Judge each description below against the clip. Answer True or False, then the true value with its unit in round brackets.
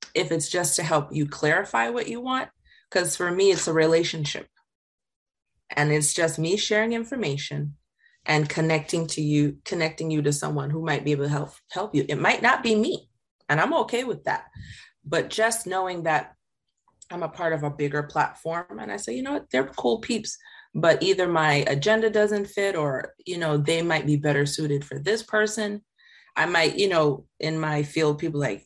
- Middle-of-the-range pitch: True (160 Hz)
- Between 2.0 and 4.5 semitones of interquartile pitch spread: False (5.3 semitones)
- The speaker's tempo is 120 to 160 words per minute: False (195 wpm)